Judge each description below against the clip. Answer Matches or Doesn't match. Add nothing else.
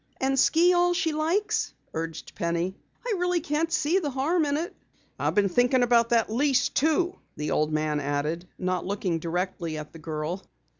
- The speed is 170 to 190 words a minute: Matches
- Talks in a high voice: Matches